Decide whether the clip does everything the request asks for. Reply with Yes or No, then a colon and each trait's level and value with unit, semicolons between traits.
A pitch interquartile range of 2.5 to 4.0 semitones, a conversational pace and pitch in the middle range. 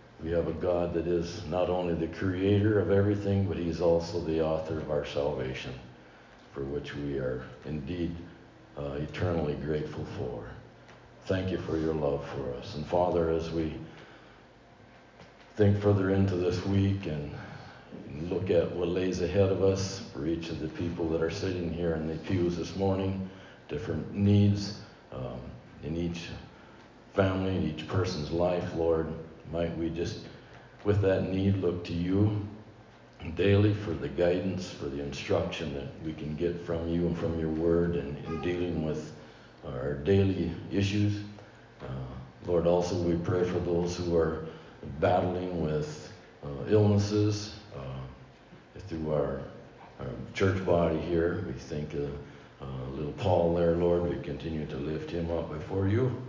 No: average, 3.4 semitones; average, 155 wpm; very low, 85 Hz